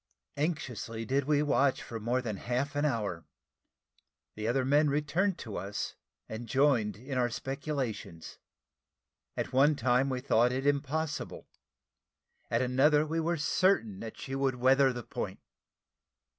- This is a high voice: No, low, 135 Hz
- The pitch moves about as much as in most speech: Yes, average, 3.6 semitones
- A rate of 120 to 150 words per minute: Yes, average, 145 wpm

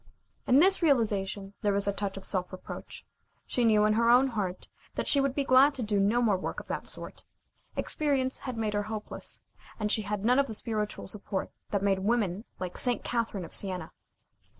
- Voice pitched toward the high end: Yes, high, 215 Hz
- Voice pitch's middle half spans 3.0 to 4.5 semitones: Yes, average, 3.7 semitones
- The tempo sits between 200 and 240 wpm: Yes, fast, 205 wpm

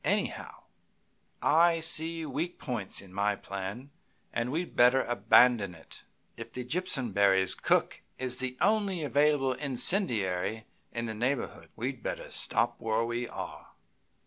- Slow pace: Yes, slow, 130 wpm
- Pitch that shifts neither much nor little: No, wide, 5.7 semitones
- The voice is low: Yes, low, 125 Hz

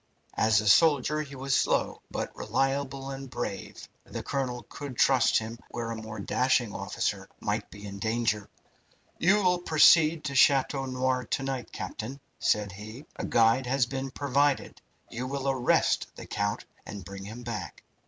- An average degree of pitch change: Yes, average, 3.7 semitones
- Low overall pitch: Yes, low, 130 Hz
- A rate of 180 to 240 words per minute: No, average, 165 wpm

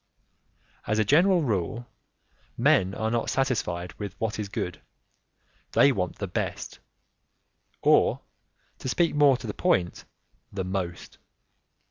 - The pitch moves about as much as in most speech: No, wide, 5.7 semitones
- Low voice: Yes, low, 110 Hz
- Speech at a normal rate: No, slow, 125 wpm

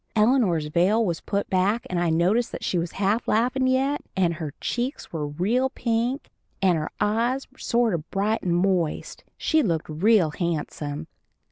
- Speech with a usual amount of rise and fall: No, wide, 5.7 semitones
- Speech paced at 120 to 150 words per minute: No, average, 165 wpm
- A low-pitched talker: No, high, 195 Hz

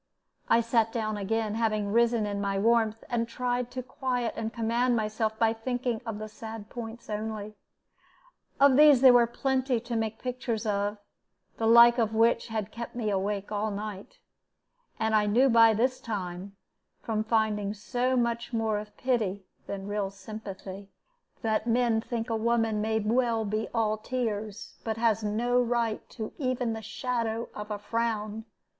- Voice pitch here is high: Yes, high, 225 Hz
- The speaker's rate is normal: Yes, average, 165 wpm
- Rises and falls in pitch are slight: Yes, narrow, 2.0 semitones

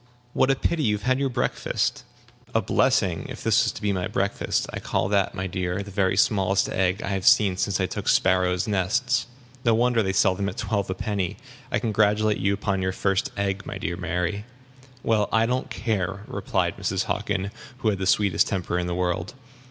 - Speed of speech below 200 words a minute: No, fast, 205 wpm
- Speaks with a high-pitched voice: No, low, 100 Hz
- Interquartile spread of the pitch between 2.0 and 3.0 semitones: Yes, narrow, 2.4 semitones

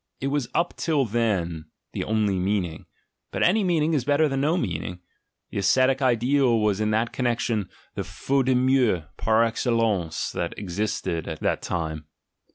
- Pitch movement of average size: No, wide, 5.8 semitones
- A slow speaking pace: No, average, 165 wpm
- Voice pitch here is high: No, low, 115 Hz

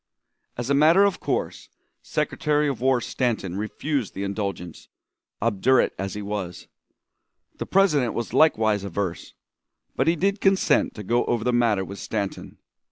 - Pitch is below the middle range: Yes, low, 115 Hz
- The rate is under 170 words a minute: Yes, average, 150 wpm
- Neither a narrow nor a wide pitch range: No, wide, 6.5 semitones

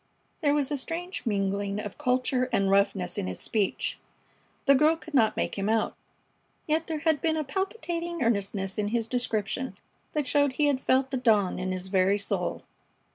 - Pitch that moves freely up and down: Yes, wide, 6.8 semitones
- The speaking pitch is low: No, very high, 250 Hz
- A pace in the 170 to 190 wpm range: Yes, average, 185 wpm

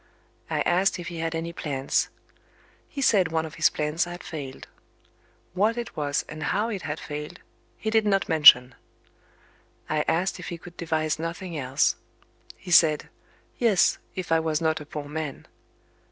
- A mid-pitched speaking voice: Yes, medium, 165 Hz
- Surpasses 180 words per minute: No, average, 170 wpm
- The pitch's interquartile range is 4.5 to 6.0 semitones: No, average, 3.0 semitones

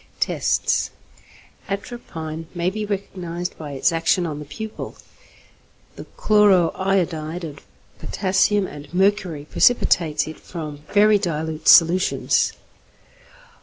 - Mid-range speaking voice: Yes, medium, 175 Hz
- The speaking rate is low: Yes, slow, 105 wpm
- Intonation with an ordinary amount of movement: Yes, average, 3.9 semitones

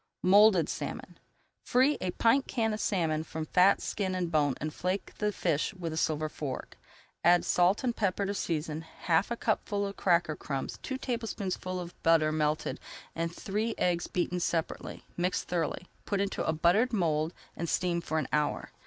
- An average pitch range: Yes, average, 4.0 semitones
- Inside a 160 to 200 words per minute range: Yes, average, 175 wpm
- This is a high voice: No, medium, 175 Hz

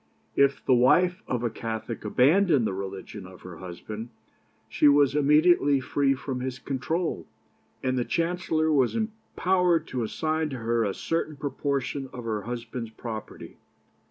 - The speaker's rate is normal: Yes, average, 150 wpm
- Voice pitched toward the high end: No, low, 135 Hz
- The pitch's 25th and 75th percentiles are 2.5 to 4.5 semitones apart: No, average, 5.3 semitones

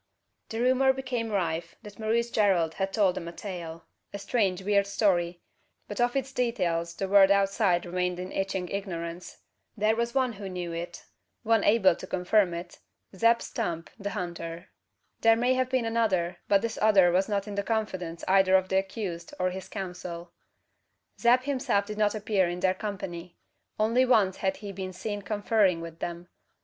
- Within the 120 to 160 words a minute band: No, average, 180 wpm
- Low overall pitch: No, high, 195 Hz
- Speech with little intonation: No, average, 3.7 semitones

